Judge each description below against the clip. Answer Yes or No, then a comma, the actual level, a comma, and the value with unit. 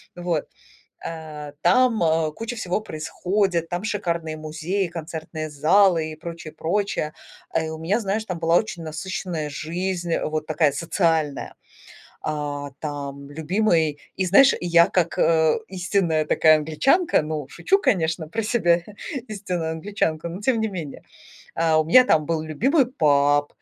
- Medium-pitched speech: Yes, medium, 165 Hz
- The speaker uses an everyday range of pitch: Yes, average, 3.7 semitones